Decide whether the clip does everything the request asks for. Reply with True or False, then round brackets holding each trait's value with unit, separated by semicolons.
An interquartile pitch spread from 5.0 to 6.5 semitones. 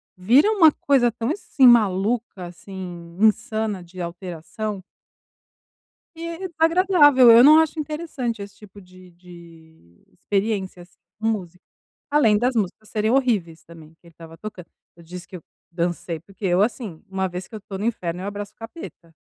True (5.3 semitones)